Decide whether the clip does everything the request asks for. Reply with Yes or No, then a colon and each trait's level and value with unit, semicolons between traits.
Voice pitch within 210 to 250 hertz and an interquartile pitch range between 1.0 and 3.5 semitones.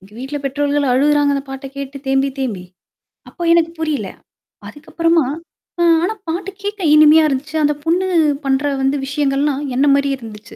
No: very high, 285 Hz; average, 2.8 semitones